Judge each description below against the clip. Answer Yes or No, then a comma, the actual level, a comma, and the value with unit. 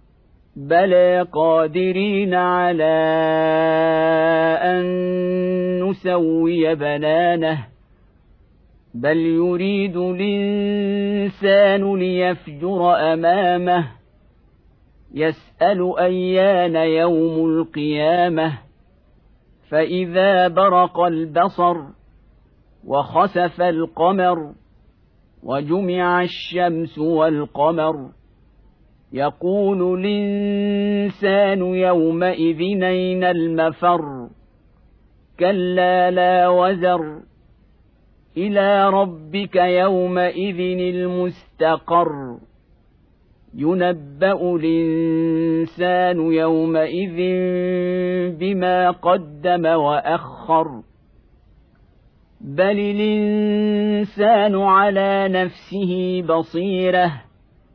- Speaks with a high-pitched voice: No, medium, 180 Hz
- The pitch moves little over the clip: Yes, narrow, 2.3 semitones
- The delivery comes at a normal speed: No, slow, 50 wpm